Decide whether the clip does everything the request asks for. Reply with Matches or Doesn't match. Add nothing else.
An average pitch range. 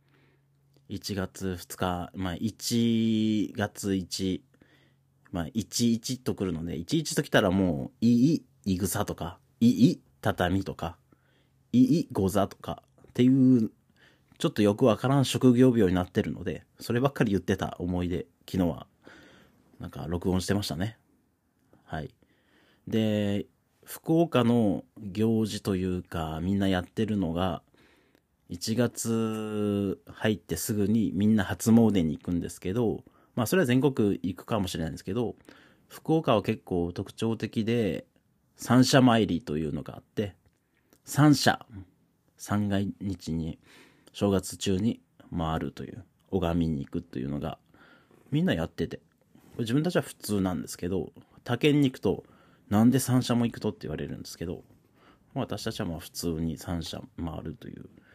Matches